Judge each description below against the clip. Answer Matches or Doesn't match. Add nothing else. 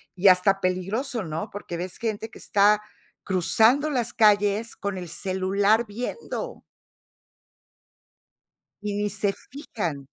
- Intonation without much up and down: Doesn't match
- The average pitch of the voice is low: Doesn't match